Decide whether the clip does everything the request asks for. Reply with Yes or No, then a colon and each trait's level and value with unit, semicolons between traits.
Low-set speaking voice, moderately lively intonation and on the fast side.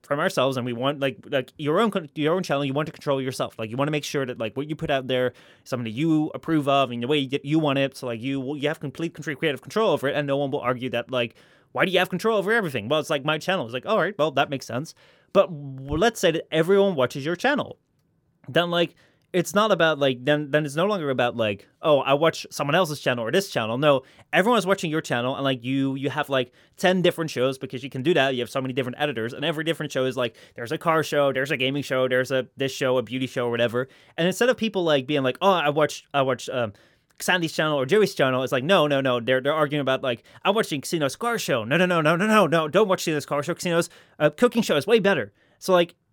No: medium, 145 Hz; average, 4.2 semitones; fast, 280 wpm